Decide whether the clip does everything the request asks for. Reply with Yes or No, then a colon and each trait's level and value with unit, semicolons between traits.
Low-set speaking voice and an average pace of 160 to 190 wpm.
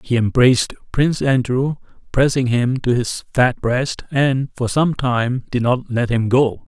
Yes: low, 125 Hz; average, 170 wpm